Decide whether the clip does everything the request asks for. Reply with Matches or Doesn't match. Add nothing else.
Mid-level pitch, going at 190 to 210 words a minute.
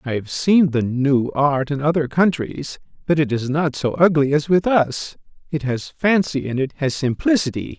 Matches